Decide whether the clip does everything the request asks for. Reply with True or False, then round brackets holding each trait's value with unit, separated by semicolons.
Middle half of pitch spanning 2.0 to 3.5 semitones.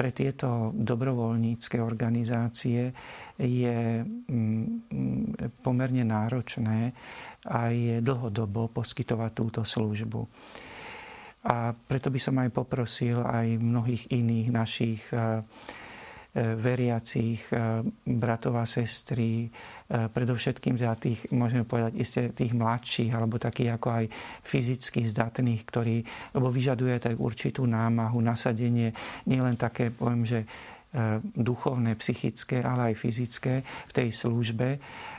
False (1.4 semitones)